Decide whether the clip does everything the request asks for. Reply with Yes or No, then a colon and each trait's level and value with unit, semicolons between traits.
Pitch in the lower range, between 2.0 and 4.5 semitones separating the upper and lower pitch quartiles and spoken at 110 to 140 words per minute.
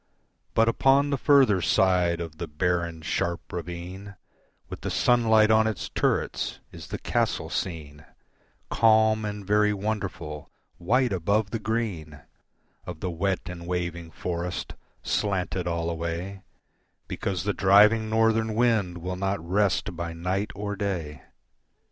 Yes: very low, 95 Hz; average, 4.0 semitones; slow, 135 wpm